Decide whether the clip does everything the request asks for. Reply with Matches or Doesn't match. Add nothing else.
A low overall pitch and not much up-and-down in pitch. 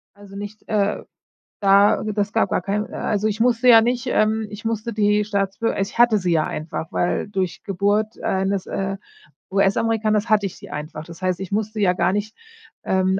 Doesn't match